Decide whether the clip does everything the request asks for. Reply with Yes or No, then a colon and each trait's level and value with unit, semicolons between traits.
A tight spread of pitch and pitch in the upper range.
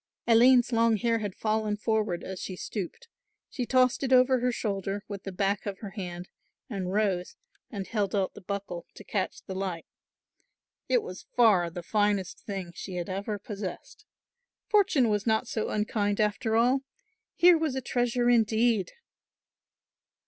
No: average, 3.5 semitones; high, 210 Hz